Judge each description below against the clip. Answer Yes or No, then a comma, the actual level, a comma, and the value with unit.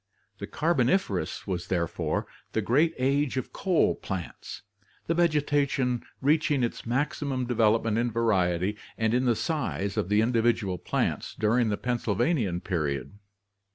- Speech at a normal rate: No, slow, 130 wpm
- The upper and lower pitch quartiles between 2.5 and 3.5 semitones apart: No, wide, 5.5 semitones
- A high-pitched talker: No, low, 120 Hz